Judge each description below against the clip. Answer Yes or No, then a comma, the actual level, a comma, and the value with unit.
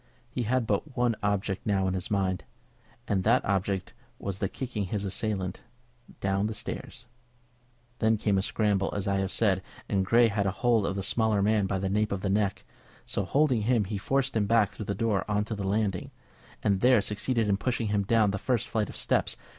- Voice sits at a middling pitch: No, low, 105 Hz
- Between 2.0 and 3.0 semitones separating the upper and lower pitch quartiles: Yes, narrow, 2.4 semitones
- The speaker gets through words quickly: Yes, fast, 210 wpm